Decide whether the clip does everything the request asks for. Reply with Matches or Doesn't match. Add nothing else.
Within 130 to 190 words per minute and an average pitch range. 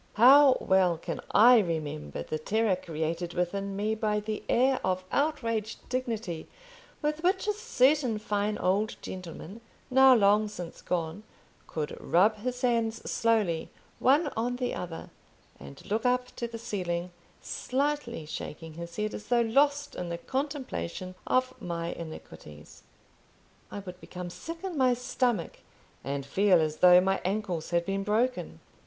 Doesn't match